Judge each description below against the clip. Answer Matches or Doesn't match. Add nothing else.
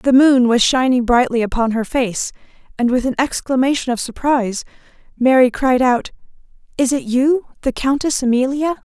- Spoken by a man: Doesn't match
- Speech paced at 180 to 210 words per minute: Doesn't match